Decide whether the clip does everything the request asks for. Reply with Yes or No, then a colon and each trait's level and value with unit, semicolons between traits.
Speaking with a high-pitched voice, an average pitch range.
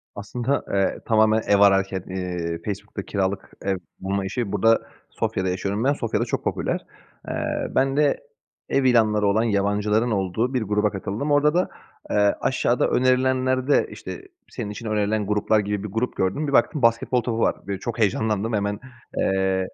No: low, 105 Hz; average, 3.6 semitones